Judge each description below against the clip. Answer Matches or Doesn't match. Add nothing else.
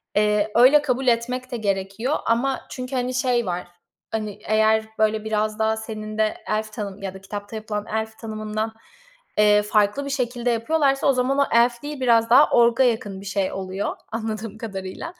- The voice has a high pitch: Matches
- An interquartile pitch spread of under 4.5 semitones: Matches